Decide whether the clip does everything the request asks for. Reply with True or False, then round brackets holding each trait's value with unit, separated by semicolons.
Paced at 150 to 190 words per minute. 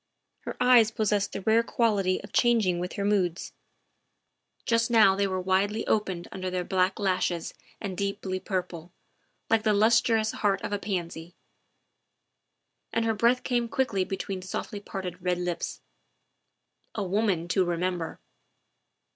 False (140 wpm)